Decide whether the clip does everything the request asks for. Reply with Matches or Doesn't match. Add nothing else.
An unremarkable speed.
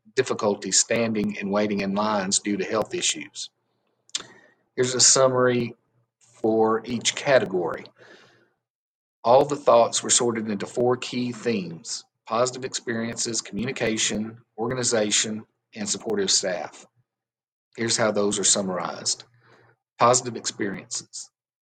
Doesn't match